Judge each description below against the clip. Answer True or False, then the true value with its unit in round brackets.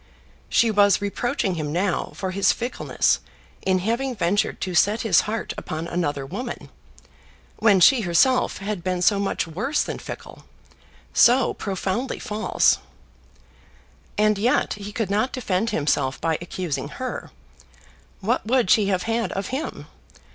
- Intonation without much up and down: False (4.1 semitones)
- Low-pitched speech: False (200 Hz)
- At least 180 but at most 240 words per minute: False (140 wpm)